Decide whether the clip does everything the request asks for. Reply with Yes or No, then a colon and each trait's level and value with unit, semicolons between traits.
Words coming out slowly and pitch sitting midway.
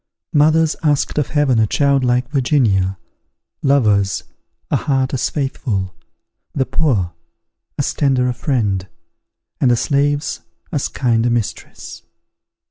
No: slow, 125 wpm; low, 130 Hz